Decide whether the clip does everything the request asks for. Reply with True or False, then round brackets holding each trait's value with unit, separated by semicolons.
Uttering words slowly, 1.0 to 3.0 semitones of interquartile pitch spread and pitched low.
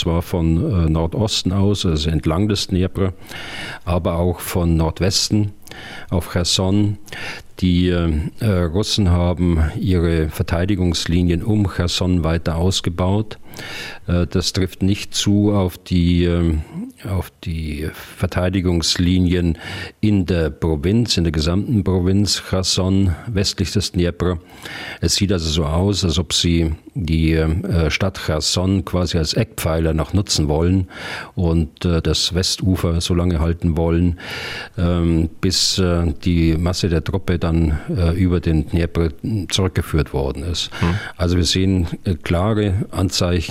True (115 wpm; 2.4 semitones; 90 Hz)